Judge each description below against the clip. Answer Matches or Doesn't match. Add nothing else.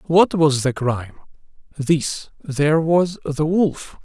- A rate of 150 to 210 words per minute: Doesn't match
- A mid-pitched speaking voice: Matches